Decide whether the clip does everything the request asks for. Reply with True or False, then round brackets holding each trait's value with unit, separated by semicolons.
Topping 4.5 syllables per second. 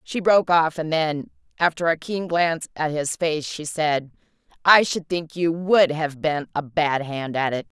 False (4.4 syllables/s)